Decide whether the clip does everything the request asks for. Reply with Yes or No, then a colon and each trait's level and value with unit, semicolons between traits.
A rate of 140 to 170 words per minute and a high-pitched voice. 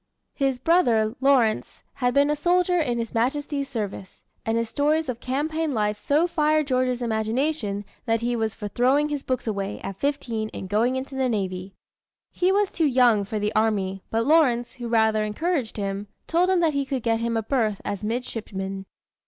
No: average, 185 wpm; high, 240 Hz